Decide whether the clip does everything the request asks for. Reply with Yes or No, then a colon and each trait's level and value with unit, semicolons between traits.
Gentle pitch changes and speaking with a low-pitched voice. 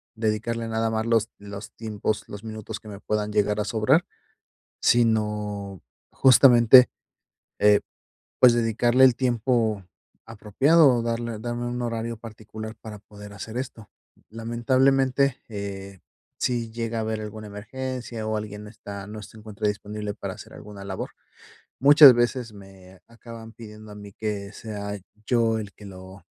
Yes: narrow, 2.2 semitones; low, 110 Hz